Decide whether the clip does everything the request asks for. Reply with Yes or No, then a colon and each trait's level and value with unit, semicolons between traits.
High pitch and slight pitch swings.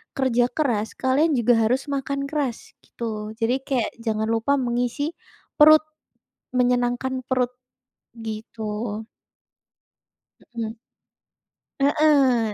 No: high, 245 Hz; average, 3.4 semitones